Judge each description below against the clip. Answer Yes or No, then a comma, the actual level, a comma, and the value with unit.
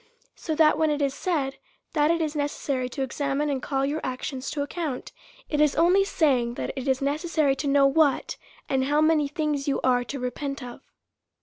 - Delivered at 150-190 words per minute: No, average, 200 wpm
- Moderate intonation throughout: No, narrow, 2.3 semitones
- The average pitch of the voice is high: Yes, very high, 285 Hz